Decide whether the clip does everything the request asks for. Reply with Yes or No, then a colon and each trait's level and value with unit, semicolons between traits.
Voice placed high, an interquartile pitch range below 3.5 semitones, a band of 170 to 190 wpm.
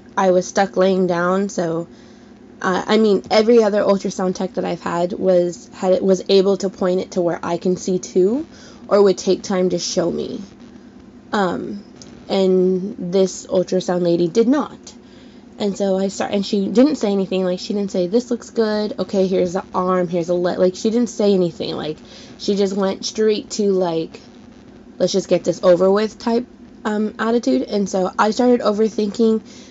Yes: high, 195 Hz; average, 2.9 semitones; average, 185 wpm